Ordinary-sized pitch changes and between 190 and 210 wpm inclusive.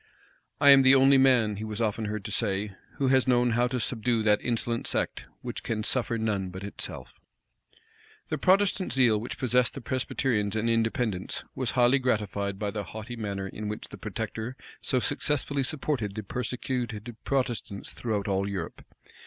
No: average, 3.5 semitones; average, 170 wpm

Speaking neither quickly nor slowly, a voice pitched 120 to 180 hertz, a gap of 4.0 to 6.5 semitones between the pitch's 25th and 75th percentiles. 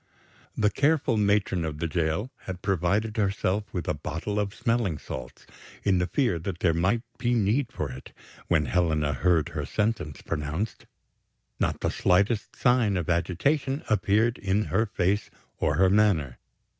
No: average, 155 wpm; very low, 95 Hz; average, 4.4 semitones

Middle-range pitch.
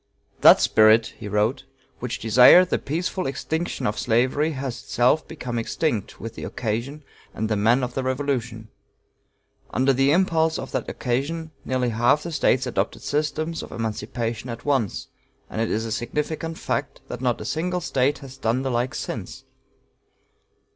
No: low, 130 Hz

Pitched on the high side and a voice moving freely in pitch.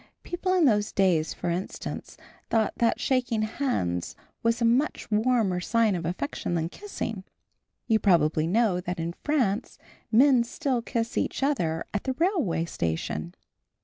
Yes: high, 215 Hz; wide, 6.5 semitones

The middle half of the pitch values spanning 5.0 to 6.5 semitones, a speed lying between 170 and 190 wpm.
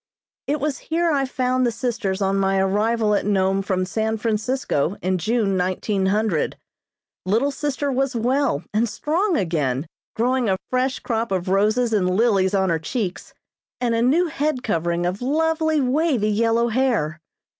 No: average, 5.3 semitones; average, 155 wpm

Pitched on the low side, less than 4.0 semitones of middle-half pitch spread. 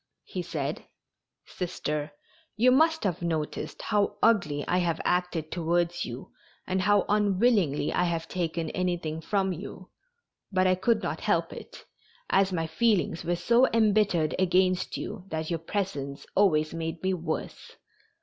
No: medium, 180 Hz; average, 3.4 semitones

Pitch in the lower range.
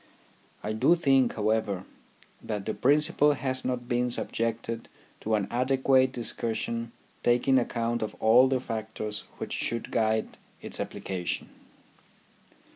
Yes: low, 115 Hz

